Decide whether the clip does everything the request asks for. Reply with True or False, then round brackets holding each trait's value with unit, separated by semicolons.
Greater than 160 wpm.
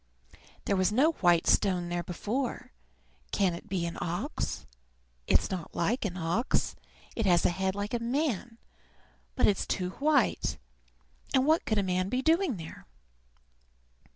False (155 wpm)